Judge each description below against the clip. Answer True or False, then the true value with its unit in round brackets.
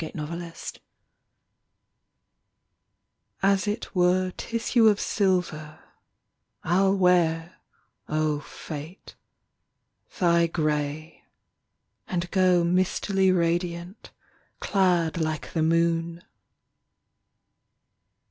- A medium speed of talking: False (75 wpm)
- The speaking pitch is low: False (170 Hz)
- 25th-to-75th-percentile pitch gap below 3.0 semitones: True (2.4 semitones)